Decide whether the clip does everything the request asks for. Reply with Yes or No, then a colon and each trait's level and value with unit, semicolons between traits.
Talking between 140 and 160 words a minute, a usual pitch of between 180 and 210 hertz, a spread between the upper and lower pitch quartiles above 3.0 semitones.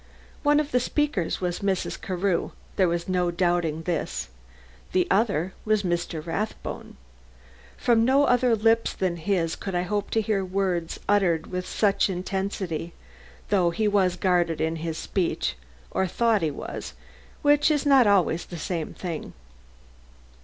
Yes: average, 150 wpm; medium, 185 Hz; average, 3.7 semitones